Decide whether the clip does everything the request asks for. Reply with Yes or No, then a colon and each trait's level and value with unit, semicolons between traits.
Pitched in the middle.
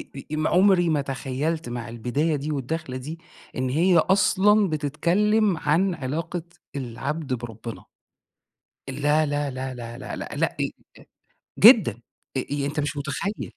Yes: medium, 150 Hz